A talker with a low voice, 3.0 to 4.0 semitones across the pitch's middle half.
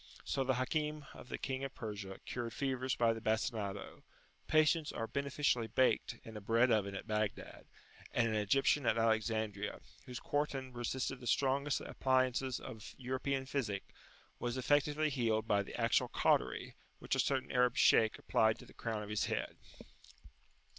Yes: low, 125 Hz; average, 3.5 semitones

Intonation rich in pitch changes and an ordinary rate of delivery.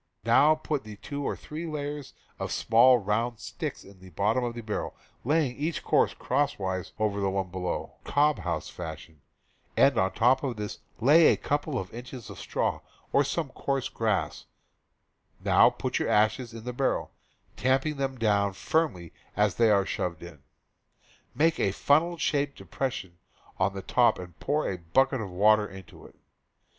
Yes: wide, 6.3 semitones; average, 170 wpm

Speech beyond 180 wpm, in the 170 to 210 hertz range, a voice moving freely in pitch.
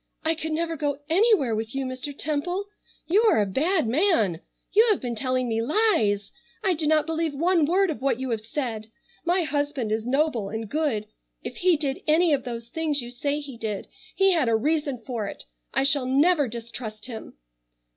No: average, 195 wpm; very high, 280 Hz; wide, 5.7 semitones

